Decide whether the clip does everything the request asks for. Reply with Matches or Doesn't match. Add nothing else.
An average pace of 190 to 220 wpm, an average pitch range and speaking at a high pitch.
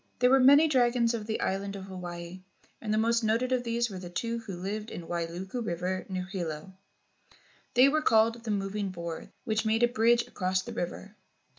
Matches